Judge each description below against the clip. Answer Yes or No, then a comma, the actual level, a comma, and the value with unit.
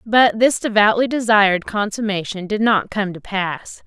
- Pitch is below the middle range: No, high, 210 Hz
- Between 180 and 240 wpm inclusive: No, average, 155 wpm